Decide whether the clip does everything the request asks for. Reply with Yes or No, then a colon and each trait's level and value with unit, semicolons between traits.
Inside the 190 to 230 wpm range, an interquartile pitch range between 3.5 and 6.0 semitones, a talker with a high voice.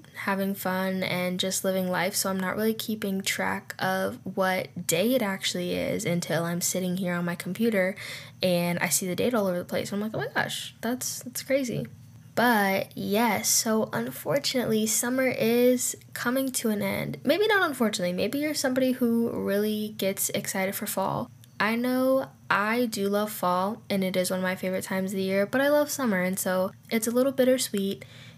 Yes: average, 195 wpm; average, 4.2 semitones; high, 195 Hz